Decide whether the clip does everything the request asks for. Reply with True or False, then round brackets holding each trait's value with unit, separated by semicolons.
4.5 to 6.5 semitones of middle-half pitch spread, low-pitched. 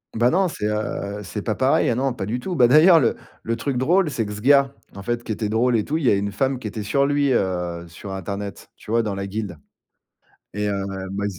True (5.0 semitones; 115 Hz)